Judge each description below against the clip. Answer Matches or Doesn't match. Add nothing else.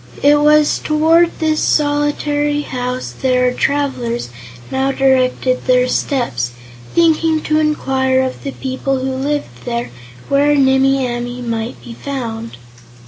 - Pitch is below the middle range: Doesn't match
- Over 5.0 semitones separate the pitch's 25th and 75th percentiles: Doesn't match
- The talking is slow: Matches